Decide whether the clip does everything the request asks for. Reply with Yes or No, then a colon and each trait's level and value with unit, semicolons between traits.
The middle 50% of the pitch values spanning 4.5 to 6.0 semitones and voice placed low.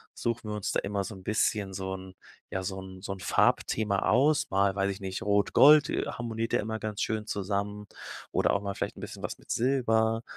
No: narrow, 2.4 semitones; low, 105 Hz